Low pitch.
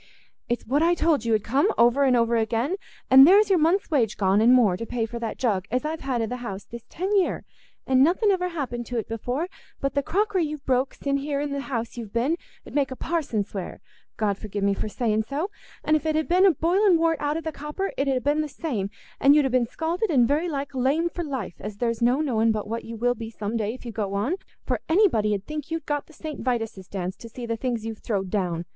No: very high, 255 Hz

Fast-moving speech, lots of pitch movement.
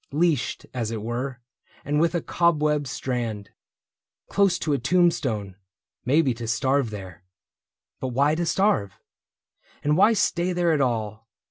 No: average, 145 wpm; wide, 6.4 semitones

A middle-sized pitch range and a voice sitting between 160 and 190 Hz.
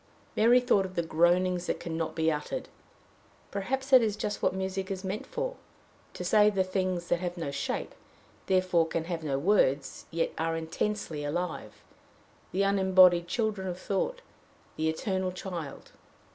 Yes: average, 3.2 semitones; medium, 185 Hz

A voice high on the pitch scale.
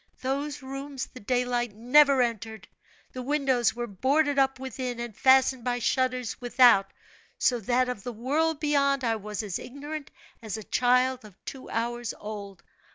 Yes: very high, 250 Hz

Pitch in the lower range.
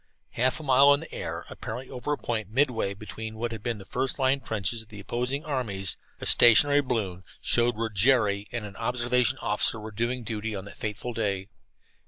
Yes: low, 115 Hz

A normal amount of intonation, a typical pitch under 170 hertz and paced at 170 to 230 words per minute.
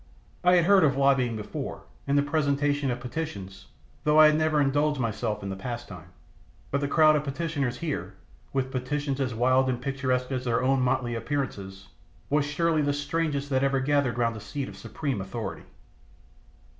Yes: average, 3.1 semitones; low, 135 Hz; average, 180 wpm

